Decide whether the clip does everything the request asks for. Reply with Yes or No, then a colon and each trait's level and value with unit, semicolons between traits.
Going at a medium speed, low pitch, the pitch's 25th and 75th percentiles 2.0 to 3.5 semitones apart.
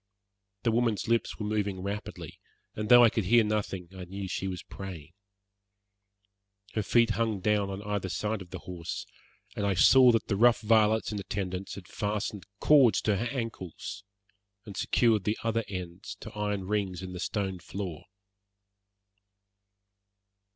Yes: average, 160 wpm; low, 105 Hz; average, 2.8 semitones